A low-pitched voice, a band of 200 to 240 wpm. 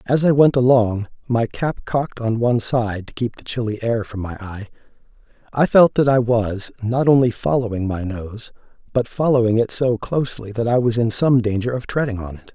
Yes: low, 115 Hz; fast, 205 wpm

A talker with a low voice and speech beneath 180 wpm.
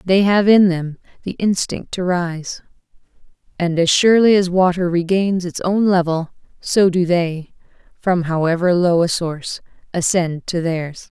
No: medium, 175 Hz; average, 150 wpm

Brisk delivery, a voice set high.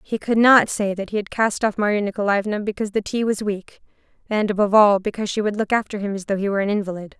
Yes: fast, 260 wpm; high, 205 Hz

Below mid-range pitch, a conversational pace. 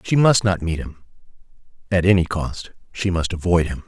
Yes: very low, 90 Hz; average, 170 wpm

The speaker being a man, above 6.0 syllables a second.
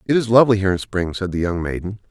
Yes: male; 7.3 syllables/s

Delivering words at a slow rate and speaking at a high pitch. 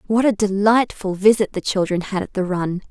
No: fast, 205 wpm; high, 200 Hz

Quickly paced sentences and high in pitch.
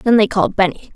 Yes: fast, 255 wpm; high, 200 Hz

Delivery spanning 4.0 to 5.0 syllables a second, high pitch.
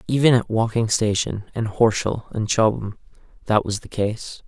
No: 4.6 syllables/s; low, 110 Hz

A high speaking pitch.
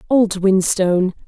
Yes: high, 195 Hz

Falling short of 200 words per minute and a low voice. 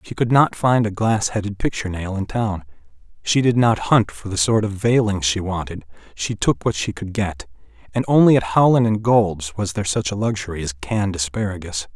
No: fast, 205 wpm; low, 100 Hz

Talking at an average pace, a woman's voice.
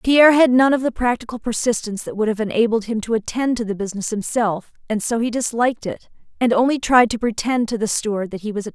No: fast, 255 wpm; female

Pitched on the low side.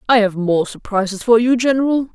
No: high, 225 Hz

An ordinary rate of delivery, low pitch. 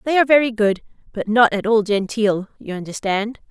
No: average, 190 wpm; high, 220 Hz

